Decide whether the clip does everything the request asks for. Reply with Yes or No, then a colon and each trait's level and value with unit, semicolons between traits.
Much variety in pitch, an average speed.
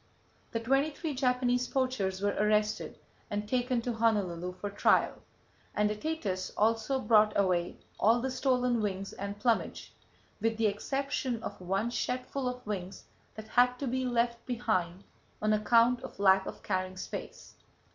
No: average, 3.7 semitones; average, 160 wpm